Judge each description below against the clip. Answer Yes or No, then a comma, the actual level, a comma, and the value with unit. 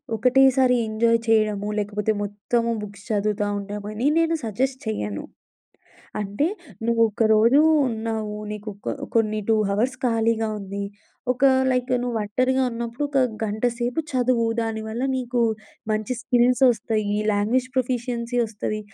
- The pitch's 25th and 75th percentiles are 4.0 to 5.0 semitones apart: No, average, 2.7 semitones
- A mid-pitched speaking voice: No, high, 225 Hz